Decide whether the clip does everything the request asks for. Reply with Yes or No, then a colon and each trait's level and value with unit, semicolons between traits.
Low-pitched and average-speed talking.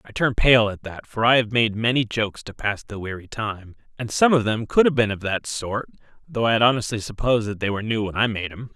No: low, 110 Hz; fast, 265 wpm